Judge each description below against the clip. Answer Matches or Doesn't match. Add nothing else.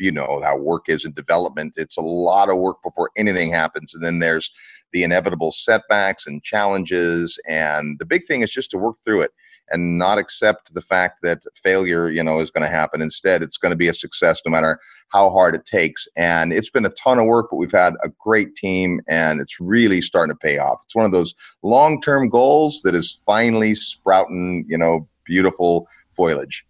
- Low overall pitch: Matches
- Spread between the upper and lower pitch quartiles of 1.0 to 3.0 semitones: Doesn't match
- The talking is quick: Matches